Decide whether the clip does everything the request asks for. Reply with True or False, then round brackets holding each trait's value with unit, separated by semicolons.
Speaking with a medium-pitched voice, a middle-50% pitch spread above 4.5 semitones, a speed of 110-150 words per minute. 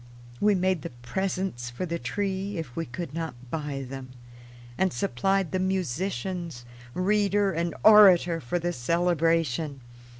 True (170 Hz; 5.1 semitones; 135 wpm)